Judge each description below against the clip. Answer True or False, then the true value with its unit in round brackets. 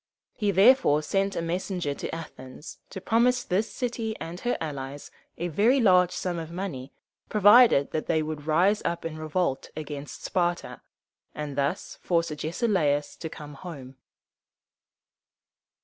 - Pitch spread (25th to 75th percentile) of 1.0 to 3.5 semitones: False (4.7 semitones)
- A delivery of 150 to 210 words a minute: False (140 wpm)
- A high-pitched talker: False (170 Hz)